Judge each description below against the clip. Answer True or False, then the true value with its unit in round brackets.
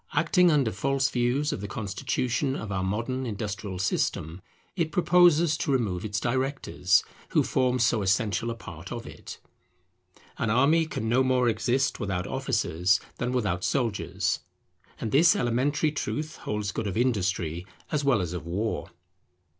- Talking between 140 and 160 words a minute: True (155 wpm)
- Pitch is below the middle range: True (120 Hz)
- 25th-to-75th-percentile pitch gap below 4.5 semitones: False (5.3 semitones)